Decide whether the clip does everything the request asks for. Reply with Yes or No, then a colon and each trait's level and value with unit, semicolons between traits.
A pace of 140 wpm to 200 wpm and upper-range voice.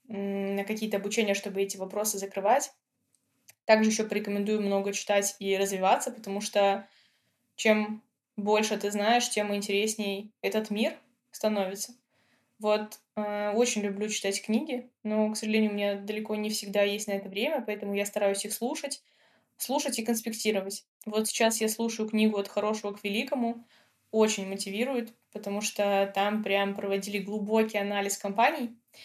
Yes: average, 145 wpm; high, 210 Hz